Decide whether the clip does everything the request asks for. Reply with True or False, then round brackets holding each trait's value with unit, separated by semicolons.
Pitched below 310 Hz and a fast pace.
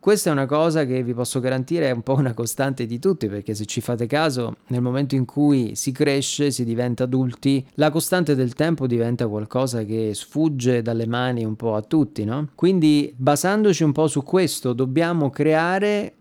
True (135 Hz; 195 wpm)